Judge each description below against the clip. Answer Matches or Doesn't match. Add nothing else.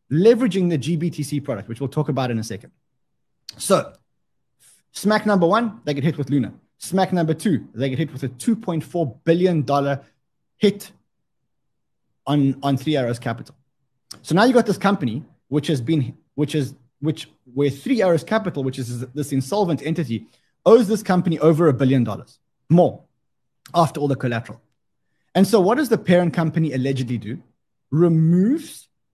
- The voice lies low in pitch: Doesn't match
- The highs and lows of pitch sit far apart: Doesn't match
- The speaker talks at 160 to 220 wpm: Matches